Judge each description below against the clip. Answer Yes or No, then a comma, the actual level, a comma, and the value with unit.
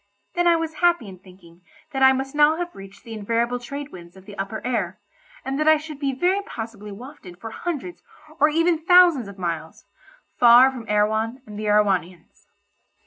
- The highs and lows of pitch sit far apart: Yes, wide, 7.1 semitones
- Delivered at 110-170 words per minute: No, average, 190 wpm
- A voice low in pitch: No, high, 235 Hz